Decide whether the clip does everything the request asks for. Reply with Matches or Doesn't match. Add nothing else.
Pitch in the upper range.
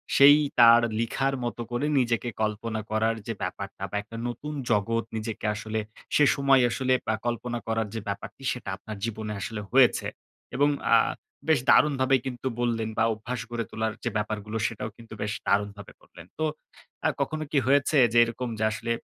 Doesn't match